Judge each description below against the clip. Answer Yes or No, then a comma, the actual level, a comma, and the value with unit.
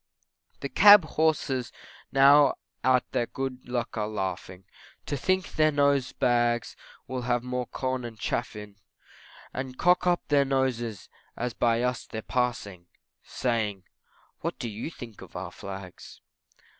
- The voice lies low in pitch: Yes, low, 125 Hz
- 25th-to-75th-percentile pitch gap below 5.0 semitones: Yes, average, 3.3 semitones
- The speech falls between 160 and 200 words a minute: No, average, 145 wpm